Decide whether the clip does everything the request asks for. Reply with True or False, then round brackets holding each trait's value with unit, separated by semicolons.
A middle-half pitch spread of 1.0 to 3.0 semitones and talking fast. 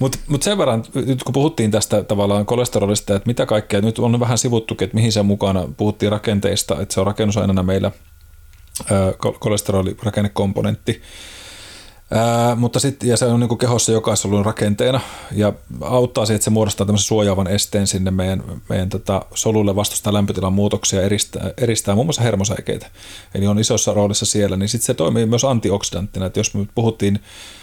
True (2.4 semitones; 165 wpm)